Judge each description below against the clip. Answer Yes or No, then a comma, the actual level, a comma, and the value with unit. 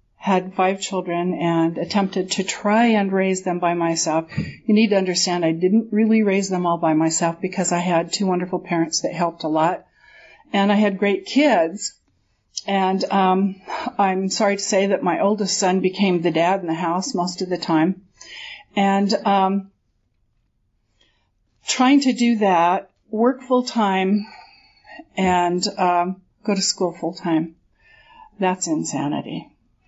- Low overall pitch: No, medium, 185 Hz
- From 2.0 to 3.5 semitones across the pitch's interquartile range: Yes, average, 2.8 semitones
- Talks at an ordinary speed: Yes, average, 155 wpm